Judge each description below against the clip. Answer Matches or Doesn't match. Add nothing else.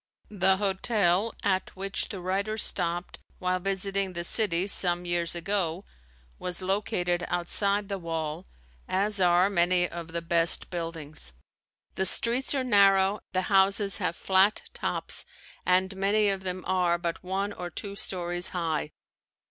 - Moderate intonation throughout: Doesn't match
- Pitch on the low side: Doesn't match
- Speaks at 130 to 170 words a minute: Matches